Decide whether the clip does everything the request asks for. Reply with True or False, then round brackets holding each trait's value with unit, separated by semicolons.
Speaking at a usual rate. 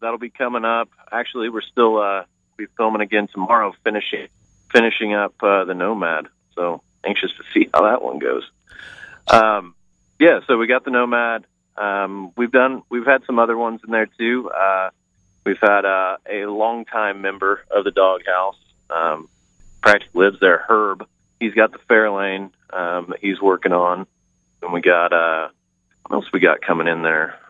True (170 wpm)